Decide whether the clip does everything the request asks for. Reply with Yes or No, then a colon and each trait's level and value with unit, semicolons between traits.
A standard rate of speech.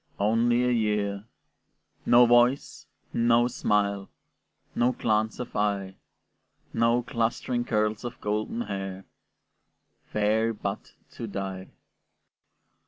No: slow, 100 wpm